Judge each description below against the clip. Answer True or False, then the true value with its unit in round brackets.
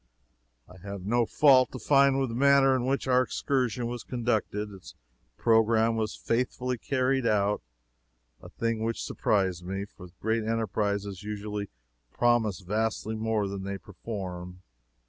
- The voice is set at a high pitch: False (110 Hz)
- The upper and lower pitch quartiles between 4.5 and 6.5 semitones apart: False (3.2 semitones)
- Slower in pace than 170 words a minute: True (145 wpm)